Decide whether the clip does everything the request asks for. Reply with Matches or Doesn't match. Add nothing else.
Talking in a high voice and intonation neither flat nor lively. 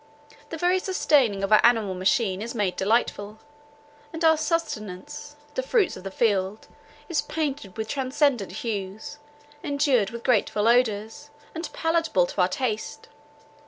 Doesn't match